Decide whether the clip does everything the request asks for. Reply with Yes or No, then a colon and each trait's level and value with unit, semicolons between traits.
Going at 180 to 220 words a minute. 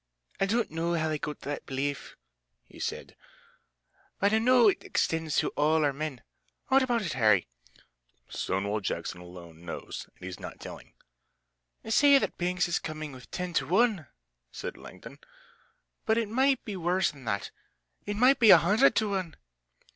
No: average, 170 wpm